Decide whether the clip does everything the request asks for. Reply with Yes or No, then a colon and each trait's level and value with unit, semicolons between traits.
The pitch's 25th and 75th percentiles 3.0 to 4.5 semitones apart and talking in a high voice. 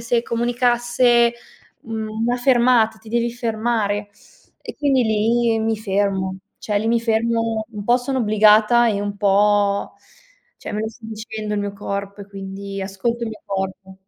No: narrow, 2.6 semitones; high, 220 Hz